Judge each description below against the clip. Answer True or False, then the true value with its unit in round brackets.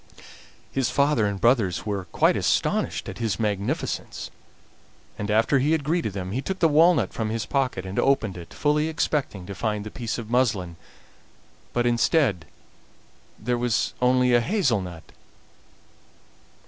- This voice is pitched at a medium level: False (115 Hz)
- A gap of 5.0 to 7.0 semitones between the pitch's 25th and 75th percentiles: True (5.4 semitones)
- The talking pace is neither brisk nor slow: True (150 wpm)